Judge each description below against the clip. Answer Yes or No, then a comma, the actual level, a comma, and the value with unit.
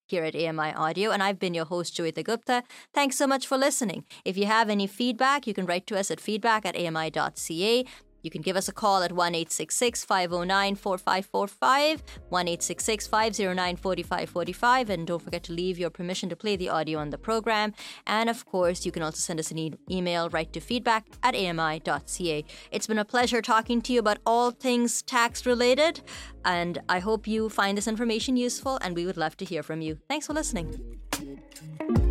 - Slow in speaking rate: No, average, 185 wpm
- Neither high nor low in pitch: No, high, 195 Hz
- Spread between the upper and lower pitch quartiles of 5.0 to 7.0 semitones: Yes, average, 5.3 semitones